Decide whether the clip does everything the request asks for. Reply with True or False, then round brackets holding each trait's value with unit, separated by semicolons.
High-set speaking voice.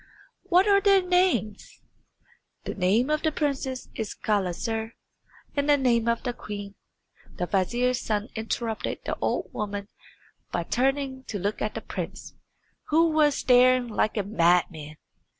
True (235 Hz)